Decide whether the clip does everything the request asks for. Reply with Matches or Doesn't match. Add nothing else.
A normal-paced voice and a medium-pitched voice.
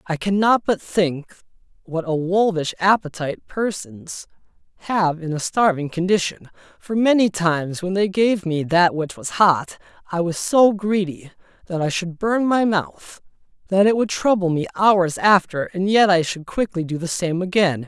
Matches